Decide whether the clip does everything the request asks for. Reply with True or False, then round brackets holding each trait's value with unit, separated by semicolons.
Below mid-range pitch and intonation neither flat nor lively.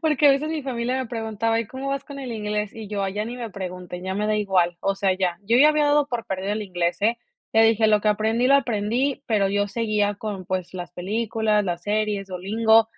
False (215 Hz; 3.1 semitones)